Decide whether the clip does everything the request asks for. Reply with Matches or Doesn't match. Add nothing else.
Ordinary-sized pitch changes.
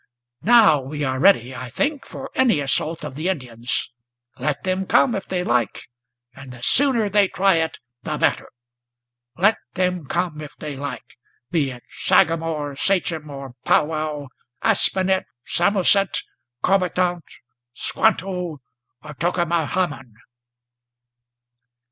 Matches